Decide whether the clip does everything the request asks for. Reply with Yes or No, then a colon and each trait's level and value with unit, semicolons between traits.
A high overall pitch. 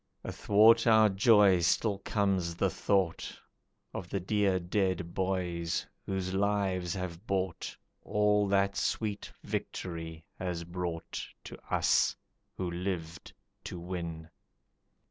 No: very low, 95 Hz